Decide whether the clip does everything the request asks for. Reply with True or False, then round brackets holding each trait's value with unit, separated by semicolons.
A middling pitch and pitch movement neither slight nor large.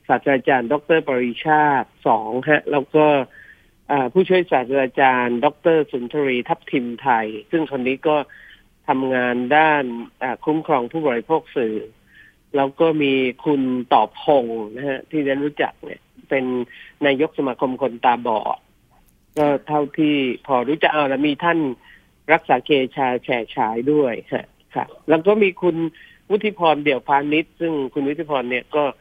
True (145 Hz; 3.2 semitones)